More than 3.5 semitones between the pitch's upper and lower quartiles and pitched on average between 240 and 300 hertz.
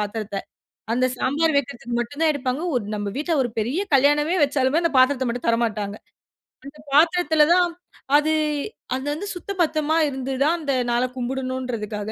Yes: average, 4.1 semitones; very high, 265 Hz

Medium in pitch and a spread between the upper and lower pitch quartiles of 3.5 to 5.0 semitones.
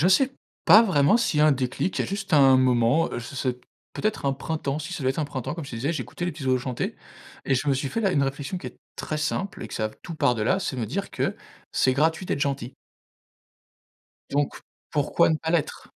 Yes: medium, 145 Hz; average, 4.5 semitones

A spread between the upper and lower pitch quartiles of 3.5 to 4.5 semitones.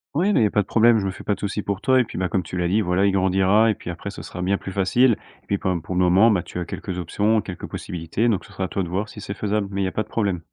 No: average, 2.7 semitones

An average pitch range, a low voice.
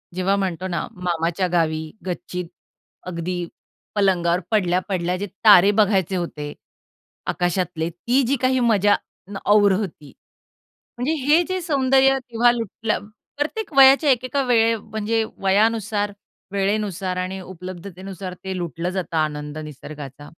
No: average, 4.3 semitones; high, 190 Hz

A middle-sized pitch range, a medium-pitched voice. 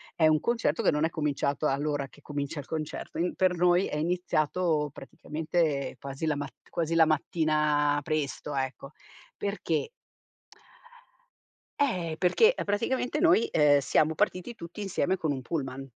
Yes: average, 3.5 semitones; medium, 155 Hz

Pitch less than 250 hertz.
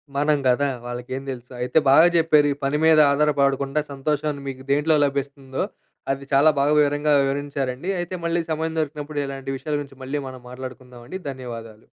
Yes: medium, 140 Hz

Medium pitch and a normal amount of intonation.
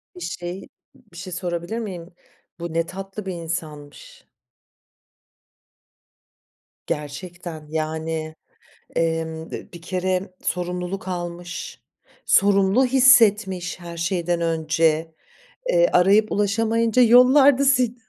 Yes: medium, 180 Hz; average, 3.6 semitones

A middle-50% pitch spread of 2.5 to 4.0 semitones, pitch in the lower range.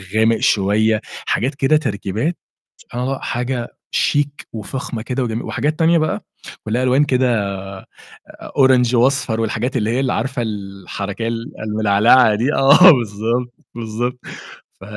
Yes: average, 3.4 semitones; low, 120 Hz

